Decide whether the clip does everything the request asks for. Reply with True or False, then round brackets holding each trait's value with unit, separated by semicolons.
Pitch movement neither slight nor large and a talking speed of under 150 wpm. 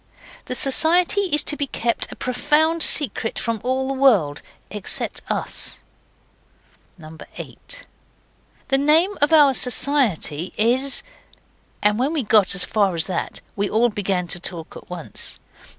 False (6.4 semitones; 140 wpm)